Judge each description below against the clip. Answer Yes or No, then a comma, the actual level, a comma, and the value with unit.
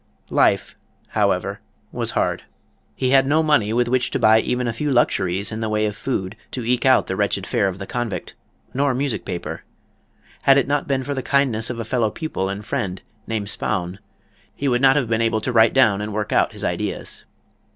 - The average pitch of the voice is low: Yes, low, 115 Hz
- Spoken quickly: Yes, fast, 210 wpm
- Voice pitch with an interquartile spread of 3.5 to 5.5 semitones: Yes, average, 4.1 semitones